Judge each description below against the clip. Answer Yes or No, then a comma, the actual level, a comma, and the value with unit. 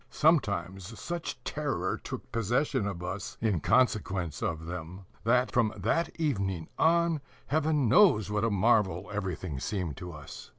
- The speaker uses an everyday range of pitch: No, wide, 5.9 semitones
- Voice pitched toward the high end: No, low, 105 Hz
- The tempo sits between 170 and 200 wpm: No, average, 140 wpm